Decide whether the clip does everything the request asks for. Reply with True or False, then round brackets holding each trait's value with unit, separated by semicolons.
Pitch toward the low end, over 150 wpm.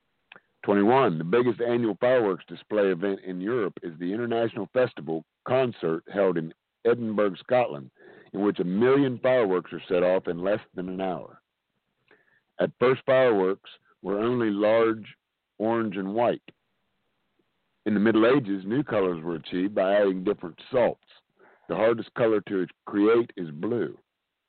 False (105 Hz; 145 wpm)